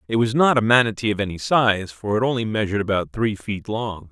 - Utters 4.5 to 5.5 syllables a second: No, 5.9 syllables/s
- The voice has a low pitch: Yes, low, 110 Hz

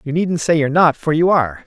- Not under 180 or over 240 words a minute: No, fast, 290 wpm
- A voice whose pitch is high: No, medium, 155 Hz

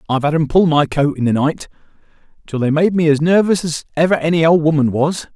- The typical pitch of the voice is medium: Yes, medium, 155 Hz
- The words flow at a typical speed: No, fast, 235 wpm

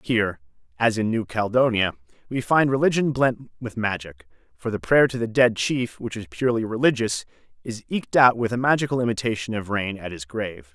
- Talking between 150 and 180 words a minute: No, average, 190 wpm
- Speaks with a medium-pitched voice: No, low, 115 Hz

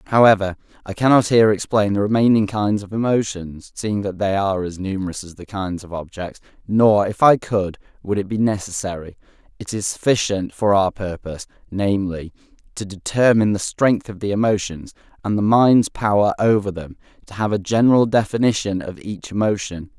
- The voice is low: Yes, low, 100 Hz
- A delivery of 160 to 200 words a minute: Yes, average, 170 wpm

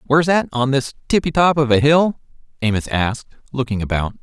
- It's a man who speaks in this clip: Yes, male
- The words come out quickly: No, average, 185 wpm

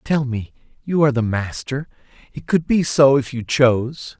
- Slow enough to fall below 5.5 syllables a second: Yes, 4.8 syllables/s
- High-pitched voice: No, low, 135 Hz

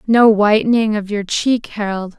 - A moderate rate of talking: Yes, average, 165 wpm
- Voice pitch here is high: Yes, high, 210 Hz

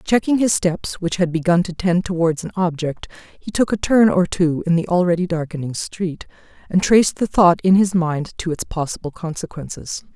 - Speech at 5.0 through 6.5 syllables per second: Yes, 5.1 syllables/s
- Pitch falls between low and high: Yes, medium, 175 Hz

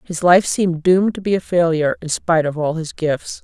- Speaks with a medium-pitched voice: Yes, medium, 170 Hz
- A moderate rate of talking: No, fast, 245 wpm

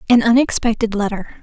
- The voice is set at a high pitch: Yes, high, 225 Hz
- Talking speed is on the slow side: Yes, slow, 125 wpm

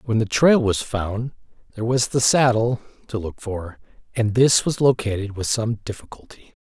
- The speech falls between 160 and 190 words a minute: Yes, average, 170 wpm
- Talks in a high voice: No, low, 115 Hz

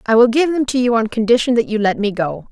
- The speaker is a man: No, female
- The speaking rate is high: Yes, fast, 310 wpm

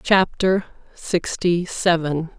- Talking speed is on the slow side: Yes, slow, 75 wpm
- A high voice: No, medium, 175 Hz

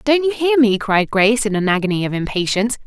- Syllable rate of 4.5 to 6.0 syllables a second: No, 6.3 syllables/s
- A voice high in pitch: Yes, high, 220 Hz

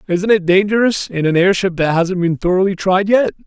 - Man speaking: Yes, male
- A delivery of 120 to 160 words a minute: No, average, 190 wpm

